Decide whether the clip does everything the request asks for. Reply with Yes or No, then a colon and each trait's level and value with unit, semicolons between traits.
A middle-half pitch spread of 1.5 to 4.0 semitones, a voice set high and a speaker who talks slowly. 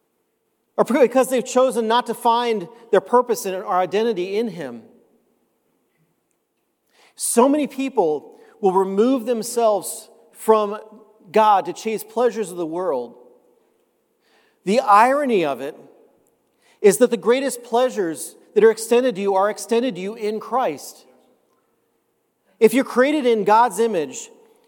Yes: average, 3.4 semitones; high, 230 Hz; slow, 130 wpm